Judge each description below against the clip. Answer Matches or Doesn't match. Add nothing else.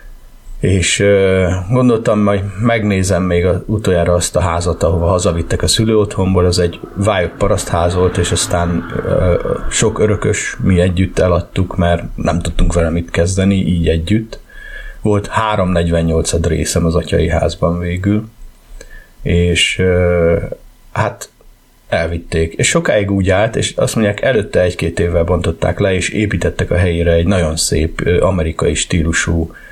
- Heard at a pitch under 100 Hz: Matches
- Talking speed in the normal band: Matches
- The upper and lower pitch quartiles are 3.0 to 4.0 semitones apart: Doesn't match